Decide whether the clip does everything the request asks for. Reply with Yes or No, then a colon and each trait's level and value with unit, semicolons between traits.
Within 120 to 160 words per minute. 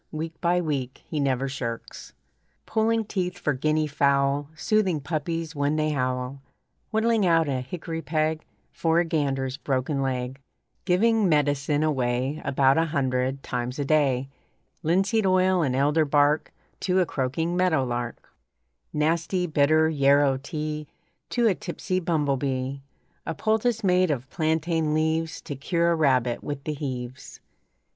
Yes: average, 140 wpm